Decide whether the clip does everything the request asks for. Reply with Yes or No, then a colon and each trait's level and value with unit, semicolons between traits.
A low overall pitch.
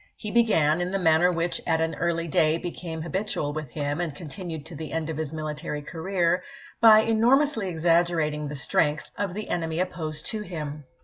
No: medium, 165 Hz